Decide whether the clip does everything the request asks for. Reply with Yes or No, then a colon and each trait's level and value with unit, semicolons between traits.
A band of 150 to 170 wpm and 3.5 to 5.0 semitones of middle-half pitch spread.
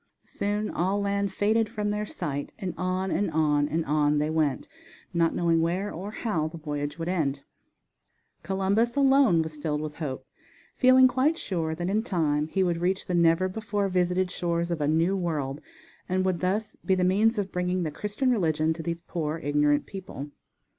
No: average, 185 wpm; average, 4.2 semitones